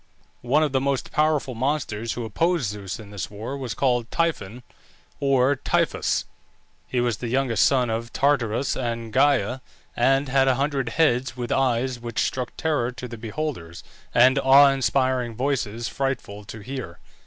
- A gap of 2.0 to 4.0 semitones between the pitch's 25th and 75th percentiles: Yes, average, 2.9 semitones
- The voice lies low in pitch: Yes, low, 125 Hz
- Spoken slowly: No, average, 160 wpm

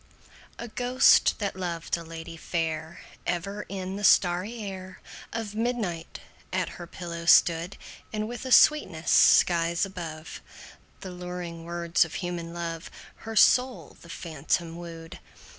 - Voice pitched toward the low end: No, medium, 175 Hz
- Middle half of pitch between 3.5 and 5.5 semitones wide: No, average, 3.1 semitones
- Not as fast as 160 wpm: Yes, slow, 135 wpm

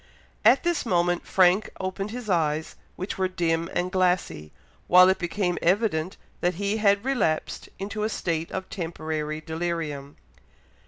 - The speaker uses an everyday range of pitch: Yes, average, 3.5 semitones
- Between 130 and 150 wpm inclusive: Yes, average, 145 wpm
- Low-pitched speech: No, medium, 180 Hz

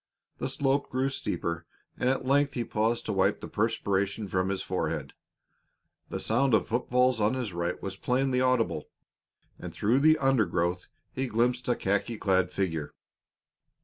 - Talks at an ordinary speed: Yes, average, 160 wpm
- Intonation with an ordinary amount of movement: Yes, average, 5.0 semitones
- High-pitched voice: No, low, 115 Hz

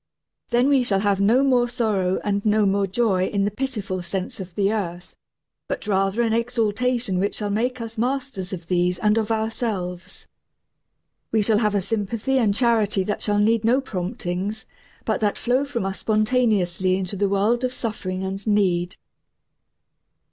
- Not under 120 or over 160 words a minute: No, average, 170 wpm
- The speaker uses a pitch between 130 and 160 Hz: No, high, 210 Hz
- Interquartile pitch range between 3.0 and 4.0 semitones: Yes, average, 3.3 semitones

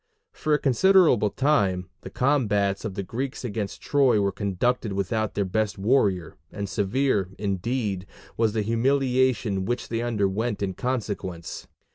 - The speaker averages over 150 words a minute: No, average, 140 wpm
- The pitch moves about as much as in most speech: Yes, average, 4.4 semitones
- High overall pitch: No, low, 110 Hz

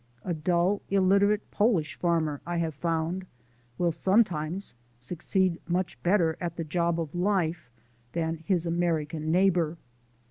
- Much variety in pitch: No, narrow, 2.5 semitones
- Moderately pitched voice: Yes, medium, 170 Hz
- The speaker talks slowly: Yes, slow, 130 wpm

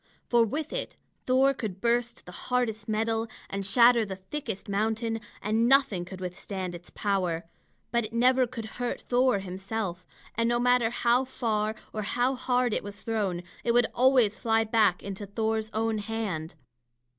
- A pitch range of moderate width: Yes, average, 3.3 semitones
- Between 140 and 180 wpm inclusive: Yes, average, 165 wpm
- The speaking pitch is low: No, high, 225 Hz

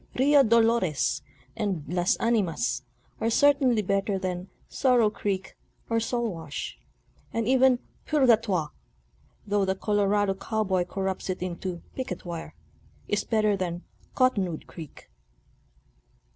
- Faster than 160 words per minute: No, slow, 135 wpm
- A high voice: Yes, high, 200 Hz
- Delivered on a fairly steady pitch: No, average, 4.4 semitones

